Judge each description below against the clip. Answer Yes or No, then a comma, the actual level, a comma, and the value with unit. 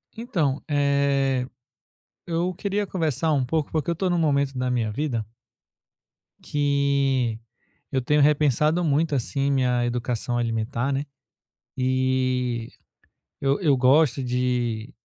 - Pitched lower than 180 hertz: Yes, low, 135 Hz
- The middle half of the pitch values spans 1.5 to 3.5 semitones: Yes, average, 3.2 semitones